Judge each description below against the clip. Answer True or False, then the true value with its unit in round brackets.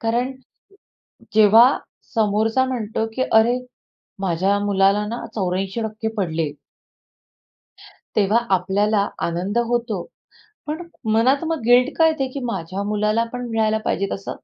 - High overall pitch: True (220 Hz)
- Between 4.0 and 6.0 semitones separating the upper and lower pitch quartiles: False (3.3 semitones)